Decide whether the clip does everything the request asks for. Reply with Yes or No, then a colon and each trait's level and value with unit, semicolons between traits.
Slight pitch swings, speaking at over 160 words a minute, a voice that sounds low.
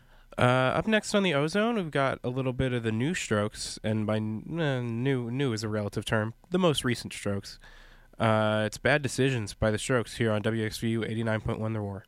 No: average, 3.6 semitones; fast, 205 wpm; low, 115 Hz